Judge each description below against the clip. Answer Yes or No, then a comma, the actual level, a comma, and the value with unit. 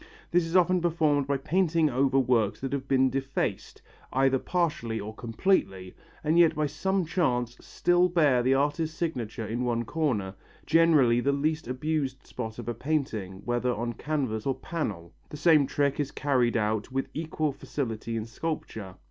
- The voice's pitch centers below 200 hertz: Yes, low, 135 Hz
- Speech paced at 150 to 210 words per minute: Yes, average, 165 wpm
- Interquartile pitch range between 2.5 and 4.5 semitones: No, average, 4.9 semitones